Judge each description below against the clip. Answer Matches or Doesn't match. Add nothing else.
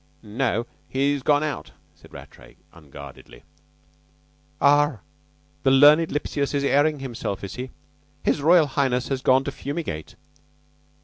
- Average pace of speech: Doesn't match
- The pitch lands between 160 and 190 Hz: Doesn't match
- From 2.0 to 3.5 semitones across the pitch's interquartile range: Matches